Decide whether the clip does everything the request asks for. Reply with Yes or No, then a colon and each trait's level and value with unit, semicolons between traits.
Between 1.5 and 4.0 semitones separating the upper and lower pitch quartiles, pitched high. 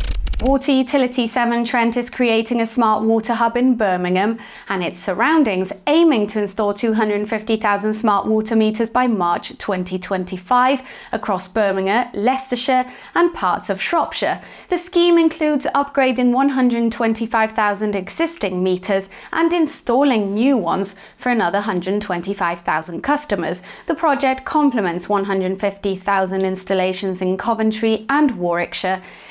No: average, 4.6 semitones; high, 220 Hz